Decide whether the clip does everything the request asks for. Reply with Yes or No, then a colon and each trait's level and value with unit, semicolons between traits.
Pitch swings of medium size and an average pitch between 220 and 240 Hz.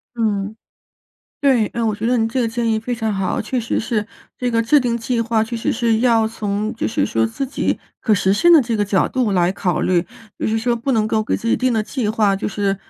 No: narrow, 2.3 semitones; high, 225 Hz